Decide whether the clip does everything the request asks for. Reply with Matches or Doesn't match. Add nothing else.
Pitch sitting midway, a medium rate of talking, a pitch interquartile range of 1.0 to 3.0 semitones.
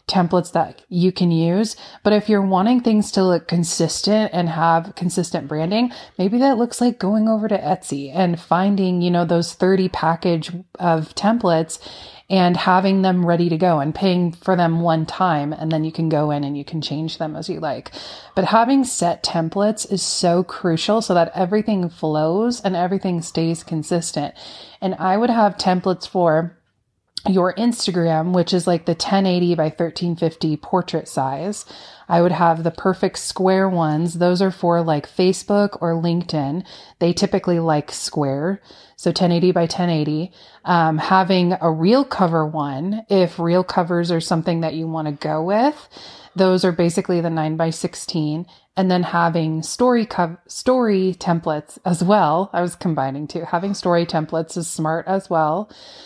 Matches